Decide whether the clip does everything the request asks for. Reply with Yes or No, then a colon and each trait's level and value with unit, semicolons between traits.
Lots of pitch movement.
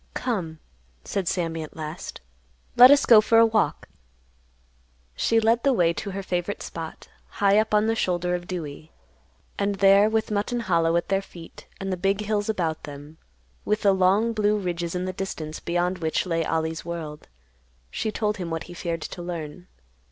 No: average, 4.1 semitones